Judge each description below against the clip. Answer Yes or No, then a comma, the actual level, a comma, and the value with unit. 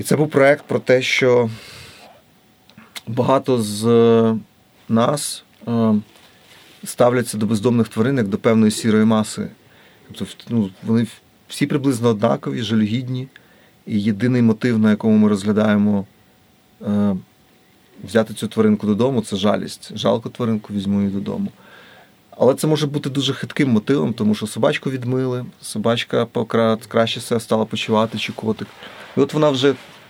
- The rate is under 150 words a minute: Yes, average, 135 wpm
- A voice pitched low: Yes, low, 115 Hz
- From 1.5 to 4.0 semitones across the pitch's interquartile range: Yes, narrow, 2.6 semitones